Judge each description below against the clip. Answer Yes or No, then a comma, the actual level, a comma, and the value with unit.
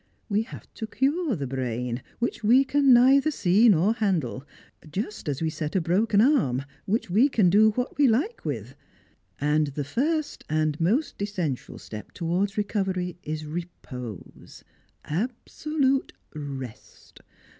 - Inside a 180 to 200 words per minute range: No, average, 145 wpm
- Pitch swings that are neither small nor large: No, wide, 8.1 semitones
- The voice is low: No, high, 190 Hz